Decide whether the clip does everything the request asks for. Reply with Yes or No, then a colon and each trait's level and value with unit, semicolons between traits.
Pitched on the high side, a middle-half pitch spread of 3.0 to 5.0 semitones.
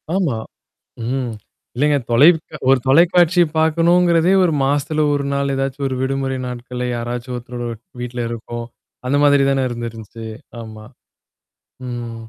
No: low, 135 Hz; average, 3.8 semitones